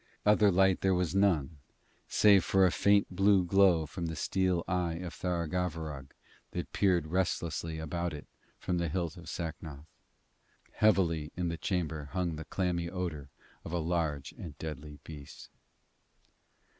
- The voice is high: No, very low, 85 Hz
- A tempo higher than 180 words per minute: No, average, 145 wpm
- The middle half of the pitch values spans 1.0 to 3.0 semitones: Yes, average, 2.7 semitones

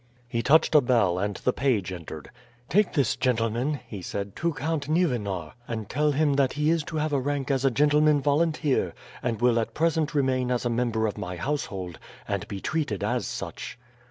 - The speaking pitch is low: Yes, low, 130 Hz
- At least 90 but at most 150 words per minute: No, average, 190 wpm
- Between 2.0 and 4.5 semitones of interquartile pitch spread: No, average, 5.3 semitones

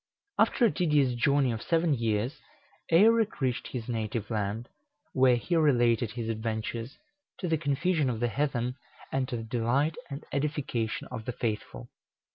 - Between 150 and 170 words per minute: Yes, average, 155 wpm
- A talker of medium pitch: No, low, 125 Hz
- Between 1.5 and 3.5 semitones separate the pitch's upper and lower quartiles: No, average, 4.4 semitones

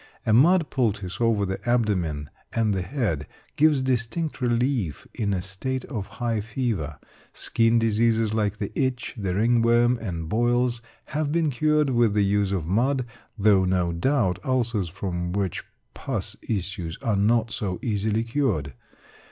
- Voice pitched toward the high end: No, low, 110 Hz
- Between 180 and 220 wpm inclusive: No, average, 150 wpm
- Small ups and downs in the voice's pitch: No, average, 4.2 semitones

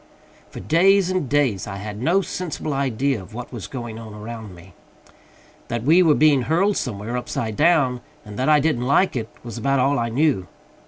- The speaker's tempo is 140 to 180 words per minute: No, average, 195 wpm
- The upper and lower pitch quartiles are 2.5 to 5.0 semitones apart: No, wide, 5.6 semitones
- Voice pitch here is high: No, low, 130 Hz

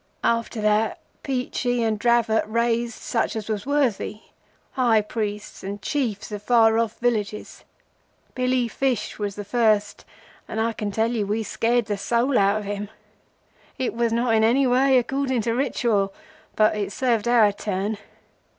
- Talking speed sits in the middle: Yes, average, 155 wpm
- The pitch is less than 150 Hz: No, high, 225 Hz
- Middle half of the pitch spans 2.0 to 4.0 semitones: Yes, narrow, 2.6 semitones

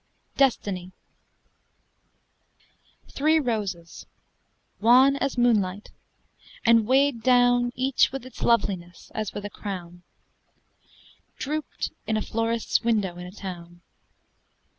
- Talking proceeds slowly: Yes, slow, 105 wpm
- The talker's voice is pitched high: Yes, high, 225 Hz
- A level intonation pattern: No, average, 5.0 semitones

